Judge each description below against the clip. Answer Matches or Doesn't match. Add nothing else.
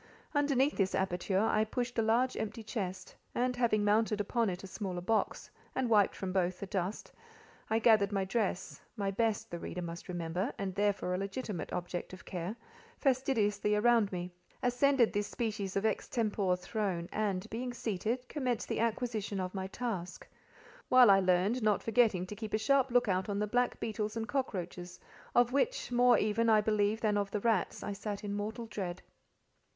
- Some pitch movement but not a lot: Matches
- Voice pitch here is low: Doesn't match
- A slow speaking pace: Doesn't match